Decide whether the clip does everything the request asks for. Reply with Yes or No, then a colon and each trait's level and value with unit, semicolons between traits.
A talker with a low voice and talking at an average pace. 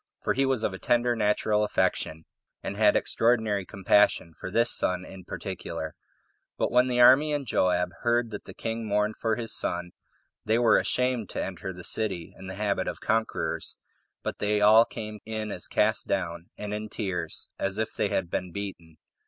Yes: low, 105 Hz; average, 185 wpm